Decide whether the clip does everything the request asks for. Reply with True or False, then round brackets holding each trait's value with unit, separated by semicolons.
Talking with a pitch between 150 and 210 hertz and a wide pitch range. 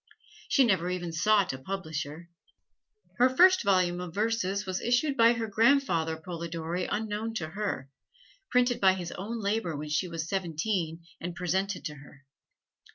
False (185 Hz; 4.8 semitones)